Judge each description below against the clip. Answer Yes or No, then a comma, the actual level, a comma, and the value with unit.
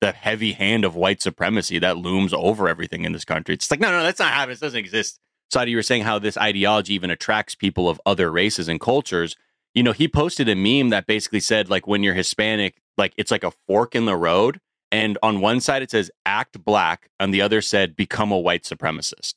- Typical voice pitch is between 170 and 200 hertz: No, low, 105 Hz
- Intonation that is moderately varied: No, narrow, 2.3 semitones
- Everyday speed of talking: No, fast, 230 wpm